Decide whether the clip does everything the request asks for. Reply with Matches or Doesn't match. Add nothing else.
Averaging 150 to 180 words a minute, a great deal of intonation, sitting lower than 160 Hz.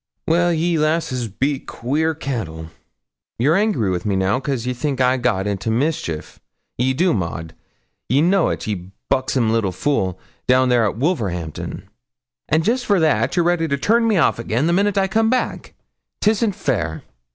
Matches